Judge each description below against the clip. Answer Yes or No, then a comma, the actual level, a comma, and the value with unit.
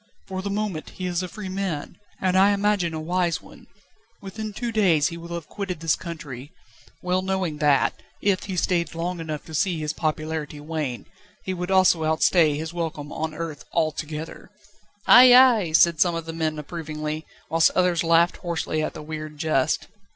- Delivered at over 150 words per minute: Yes, average, 180 wpm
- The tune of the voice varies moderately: Yes, average, 3.1 semitones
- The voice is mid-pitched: Yes, medium, 165 Hz